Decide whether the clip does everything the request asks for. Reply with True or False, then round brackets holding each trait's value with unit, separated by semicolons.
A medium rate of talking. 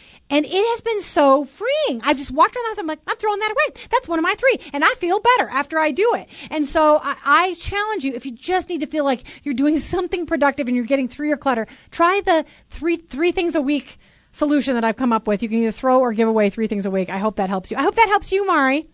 False (285 wpm)